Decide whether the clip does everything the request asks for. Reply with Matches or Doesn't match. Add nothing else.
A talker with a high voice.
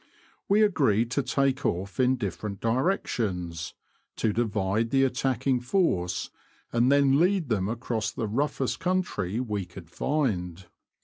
Doesn't match